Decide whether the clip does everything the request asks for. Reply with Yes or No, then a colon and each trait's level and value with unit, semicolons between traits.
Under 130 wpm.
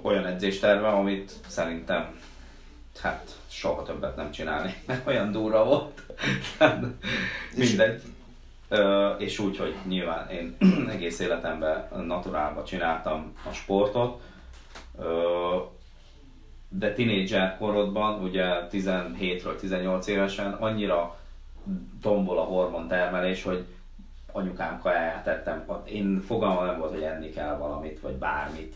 Yes: slow, 105 wpm